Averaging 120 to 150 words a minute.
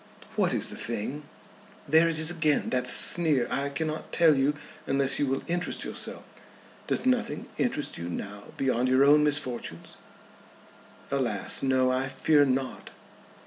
Yes: average, 145 wpm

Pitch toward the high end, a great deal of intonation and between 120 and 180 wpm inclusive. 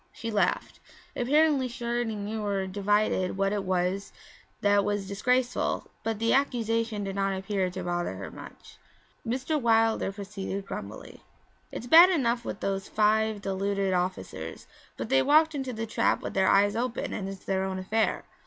No: high, 205 Hz; average, 3.3 semitones; average, 165 wpm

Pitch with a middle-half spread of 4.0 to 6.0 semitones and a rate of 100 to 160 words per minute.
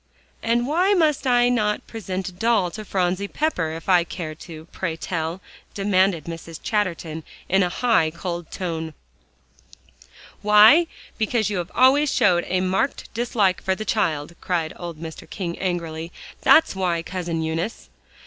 Yes: average, 4.5 semitones; average, 150 wpm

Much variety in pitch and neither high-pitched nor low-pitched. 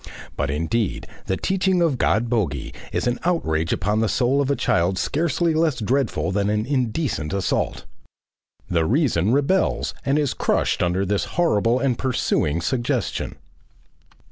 No: wide, 6.8 semitones; low, 120 Hz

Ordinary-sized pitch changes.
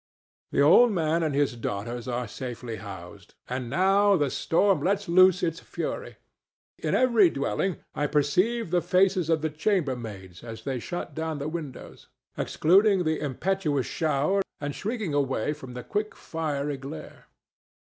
No: wide, 6.1 semitones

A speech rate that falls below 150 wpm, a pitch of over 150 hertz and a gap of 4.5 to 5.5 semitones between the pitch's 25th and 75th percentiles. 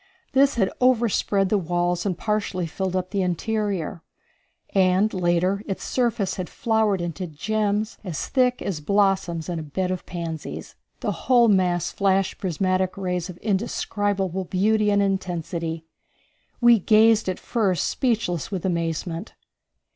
No: average, 140 wpm; high, 190 Hz; average, 3.2 semitones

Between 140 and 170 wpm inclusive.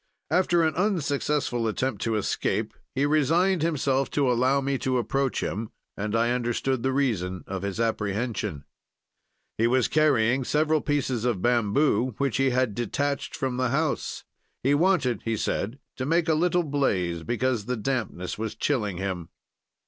Yes: average, 155 wpm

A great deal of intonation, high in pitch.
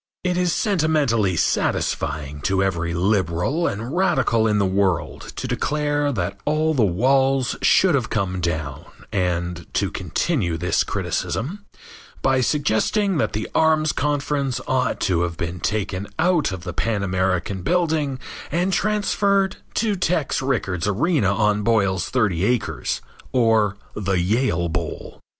No: wide, 8.2 semitones; low, 110 Hz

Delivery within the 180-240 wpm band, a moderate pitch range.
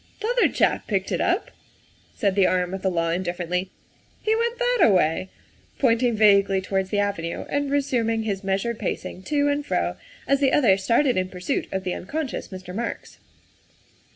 No: average, 190 wpm; wide, 6.9 semitones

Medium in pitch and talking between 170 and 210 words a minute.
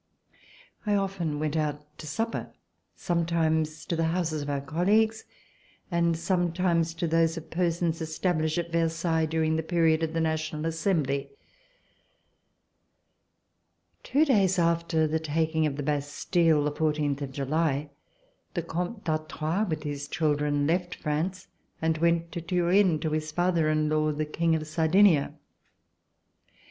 No: medium, 160 Hz; average, 140 wpm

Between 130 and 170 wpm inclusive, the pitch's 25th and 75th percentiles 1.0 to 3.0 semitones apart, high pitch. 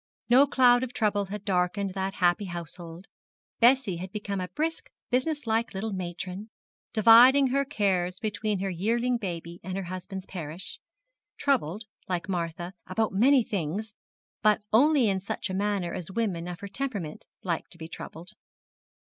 No: average, 155 wpm; average, 4.3 semitones; high, 200 Hz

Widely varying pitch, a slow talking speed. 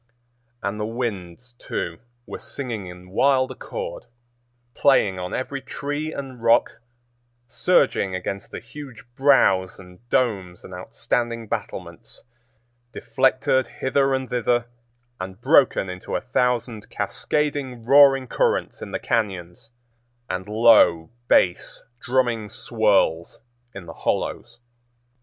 Yes: wide, 5.7 semitones; slow, 115 wpm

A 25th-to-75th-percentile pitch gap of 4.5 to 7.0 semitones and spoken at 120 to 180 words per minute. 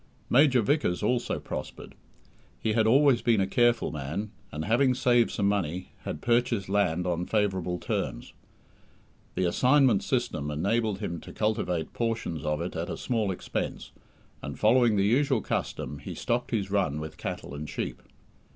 Yes: average, 5.3 semitones; average, 160 wpm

